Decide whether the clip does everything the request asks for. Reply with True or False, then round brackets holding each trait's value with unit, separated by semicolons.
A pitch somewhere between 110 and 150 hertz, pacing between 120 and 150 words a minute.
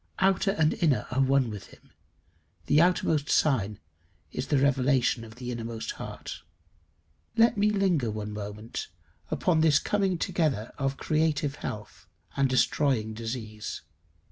True (135 Hz; 135 wpm)